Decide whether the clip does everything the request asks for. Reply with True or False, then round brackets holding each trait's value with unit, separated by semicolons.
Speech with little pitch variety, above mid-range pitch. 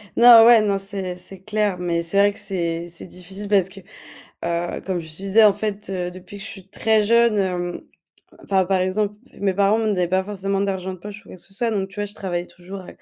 True (2.3 semitones; 195 Hz)